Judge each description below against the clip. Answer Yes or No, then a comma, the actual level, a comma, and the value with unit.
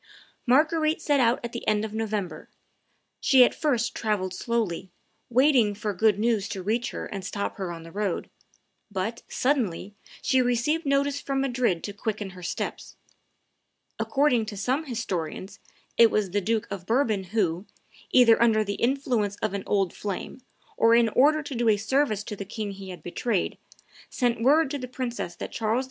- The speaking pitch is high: Yes, high, 225 Hz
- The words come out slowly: No, average, 180 wpm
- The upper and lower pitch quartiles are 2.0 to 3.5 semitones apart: No, average, 4.1 semitones